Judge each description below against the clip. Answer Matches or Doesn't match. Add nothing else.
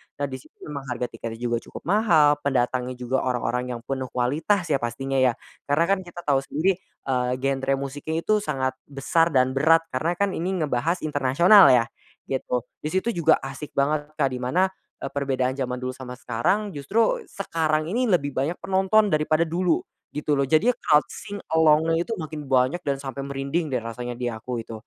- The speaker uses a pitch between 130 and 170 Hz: Matches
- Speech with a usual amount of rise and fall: Matches